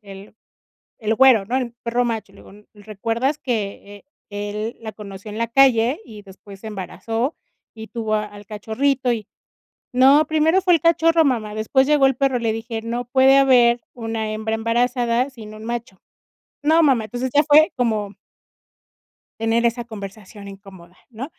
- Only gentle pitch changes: No, average, 3.6 semitones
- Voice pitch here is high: Yes, high, 230 Hz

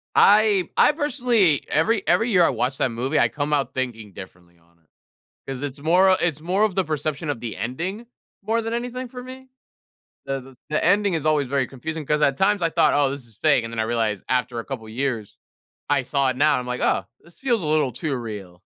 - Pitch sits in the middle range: Yes, medium, 145 Hz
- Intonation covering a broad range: Yes, wide, 7.2 semitones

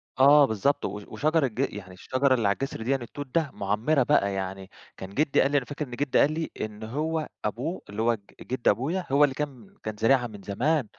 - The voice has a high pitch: No, low, 130 Hz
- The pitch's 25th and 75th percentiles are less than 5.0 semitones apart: No, average, 5.3 semitones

